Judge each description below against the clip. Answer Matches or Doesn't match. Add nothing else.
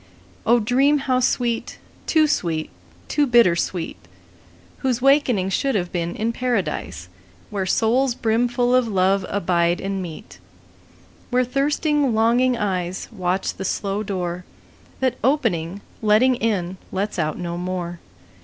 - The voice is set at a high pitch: Matches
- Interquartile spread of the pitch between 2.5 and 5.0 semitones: Doesn't match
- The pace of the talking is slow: Matches